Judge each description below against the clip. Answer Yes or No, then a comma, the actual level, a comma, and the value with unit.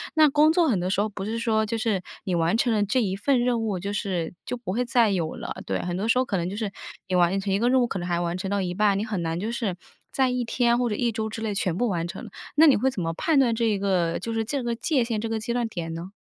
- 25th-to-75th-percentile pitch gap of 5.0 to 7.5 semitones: No, average, 4.2 semitones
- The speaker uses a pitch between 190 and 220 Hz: Yes, high, 215 Hz